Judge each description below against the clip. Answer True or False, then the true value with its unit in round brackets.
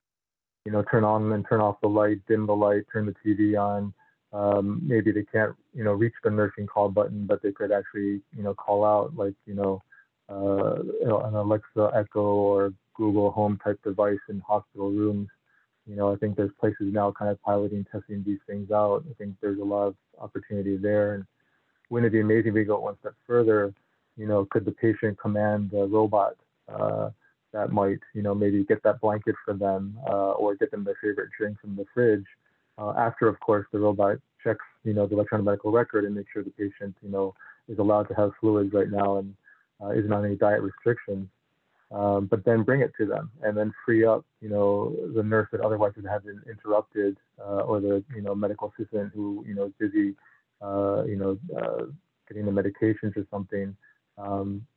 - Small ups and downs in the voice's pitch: True (1.1 semitones)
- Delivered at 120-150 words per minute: False (205 wpm)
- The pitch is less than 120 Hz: True (105 Hz)